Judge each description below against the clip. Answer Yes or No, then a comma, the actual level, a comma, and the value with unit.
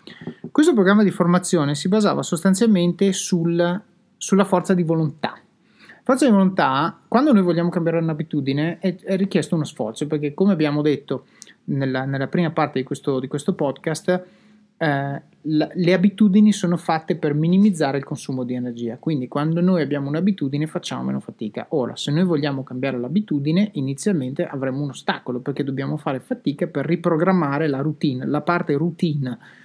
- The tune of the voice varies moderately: Yes, average, 4.6 semitones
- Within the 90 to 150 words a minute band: No, average, 160 wpm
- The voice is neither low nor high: Yes, medium, 165 Hz